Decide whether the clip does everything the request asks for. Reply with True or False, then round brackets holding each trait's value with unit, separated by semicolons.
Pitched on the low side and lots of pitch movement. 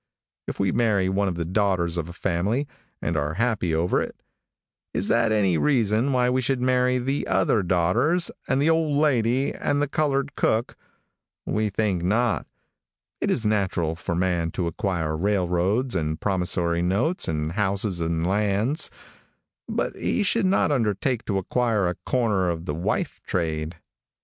True (100 Hz; 6.2 semitones)